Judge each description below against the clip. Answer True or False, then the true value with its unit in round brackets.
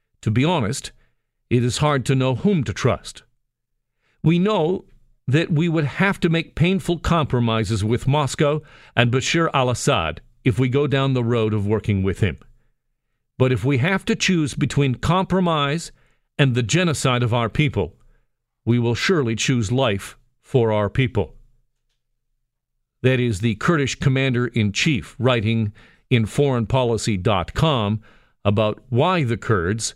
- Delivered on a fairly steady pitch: False (4.3 semitones)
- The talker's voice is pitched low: True (125 Hz)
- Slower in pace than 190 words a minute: True (145 wpm)